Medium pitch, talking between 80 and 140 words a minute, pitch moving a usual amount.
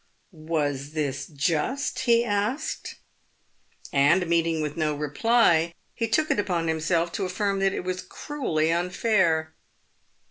Yes: medium, 170 Hz; slow, 135 wpm; average, 4.6 semitones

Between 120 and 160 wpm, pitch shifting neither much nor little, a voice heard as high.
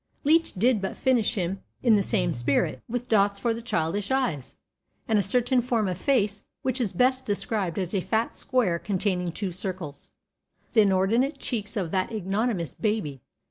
No: average, 175 wpm; average, 4.4 semitones; high, 205 Hz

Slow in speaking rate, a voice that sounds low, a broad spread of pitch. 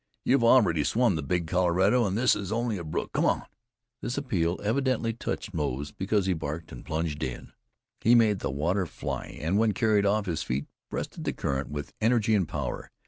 No: average, 195 wpm; very low, 95 Hz; wide, 6.0 semitones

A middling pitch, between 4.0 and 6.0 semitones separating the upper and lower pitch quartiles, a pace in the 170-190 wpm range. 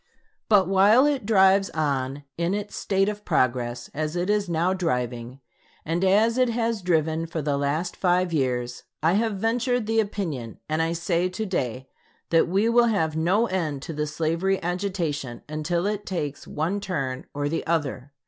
Yes: medium, 170 Hz; average, 5.3 semitones; average, 175 wpm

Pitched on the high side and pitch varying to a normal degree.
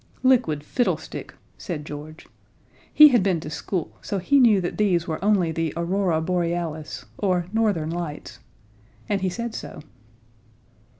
No: medium, 175 Hz; average, 4.3 semitones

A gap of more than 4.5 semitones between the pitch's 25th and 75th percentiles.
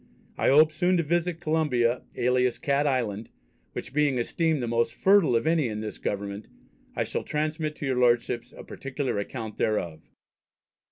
Yes: average, 4.9 semitones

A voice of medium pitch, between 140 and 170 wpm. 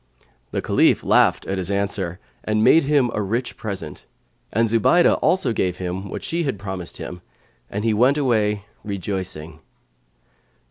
No: low, 105 Hz; average, 150 wpm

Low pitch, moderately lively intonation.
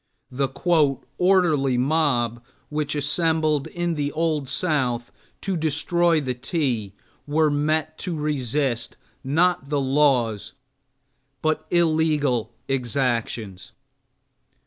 No: medium, 145 Hz; average, 3.8 semitones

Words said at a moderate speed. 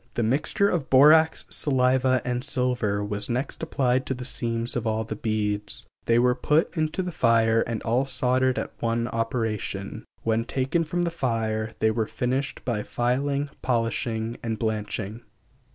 Yes: average, 160 wpm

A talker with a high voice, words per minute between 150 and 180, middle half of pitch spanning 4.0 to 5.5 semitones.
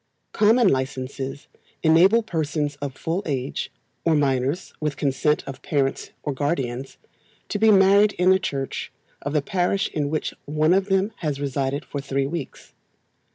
No: medium, 150 Hz; average, 155 wpm; average, 4.9 semitones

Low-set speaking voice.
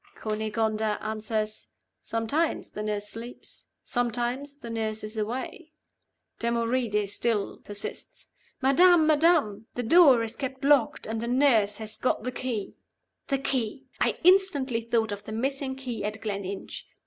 No: high, 230 Hz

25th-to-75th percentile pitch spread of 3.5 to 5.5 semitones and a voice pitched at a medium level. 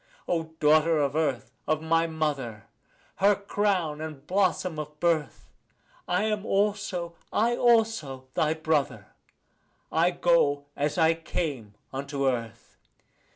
Yes: average, 3.8 semitones; medium, 160 Hz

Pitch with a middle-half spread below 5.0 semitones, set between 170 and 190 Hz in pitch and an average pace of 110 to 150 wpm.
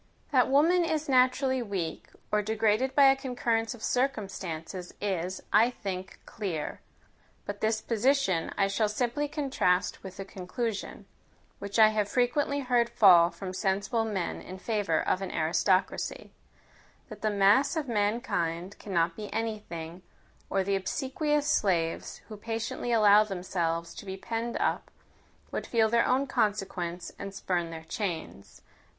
No: average, 4.5 semitones; high, 210 Hz; average, 145 wpm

